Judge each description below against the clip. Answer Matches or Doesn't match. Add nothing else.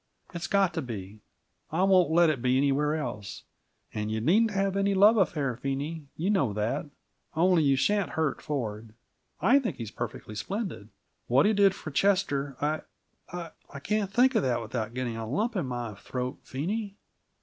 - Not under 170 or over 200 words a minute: Matches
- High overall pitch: Doesn't match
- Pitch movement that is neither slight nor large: Doesn't match